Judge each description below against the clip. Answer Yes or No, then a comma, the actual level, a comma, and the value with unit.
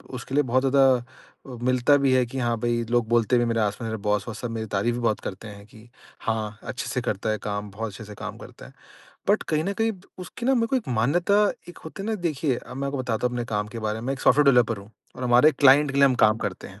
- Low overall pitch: Yes, low, 120 Hz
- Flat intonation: No, average, 3.8 semitones